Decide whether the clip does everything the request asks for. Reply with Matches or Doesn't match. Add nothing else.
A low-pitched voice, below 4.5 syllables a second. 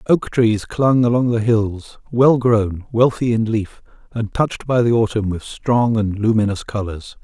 Matches